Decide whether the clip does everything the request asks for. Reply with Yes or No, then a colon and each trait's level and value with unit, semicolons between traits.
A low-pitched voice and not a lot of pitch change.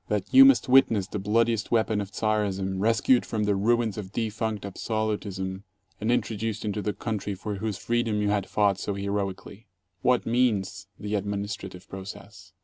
Yes: low, 105 Hz; narrow, 2.2 semitones